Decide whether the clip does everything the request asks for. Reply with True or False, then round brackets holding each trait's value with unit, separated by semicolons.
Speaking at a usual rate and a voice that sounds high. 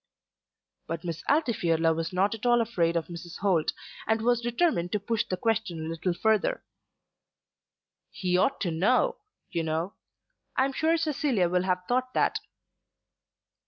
True (155 wpm; 195 Hz)